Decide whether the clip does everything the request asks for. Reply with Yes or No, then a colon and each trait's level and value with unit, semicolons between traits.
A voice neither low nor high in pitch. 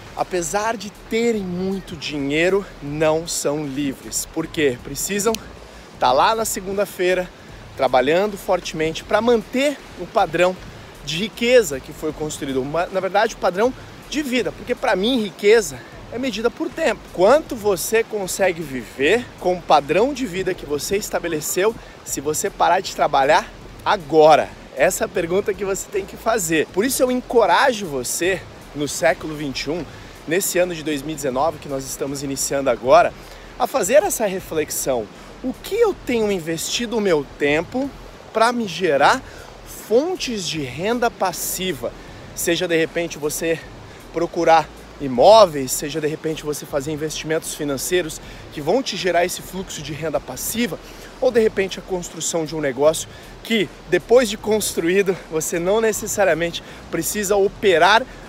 Yes: medium, 180 Hz